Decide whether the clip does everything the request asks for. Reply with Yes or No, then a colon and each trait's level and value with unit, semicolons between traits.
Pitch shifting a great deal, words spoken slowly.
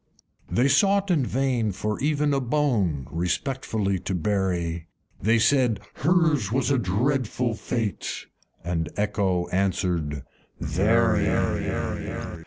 Yes: wide, 6.6 semitones; slow, 110 wpm